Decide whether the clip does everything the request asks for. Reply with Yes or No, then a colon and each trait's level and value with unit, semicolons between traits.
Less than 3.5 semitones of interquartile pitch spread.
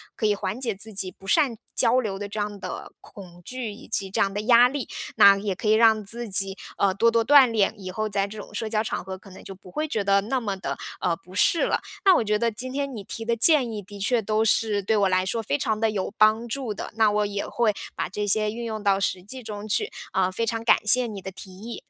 Yes: average, 2.7 semitones